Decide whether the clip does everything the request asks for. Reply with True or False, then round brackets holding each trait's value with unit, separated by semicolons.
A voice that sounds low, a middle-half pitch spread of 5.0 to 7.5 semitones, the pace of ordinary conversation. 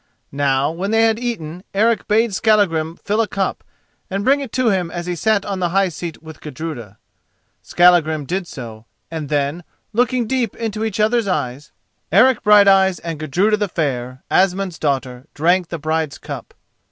False (180 Hz; 5.3 semitones; 170 wpm)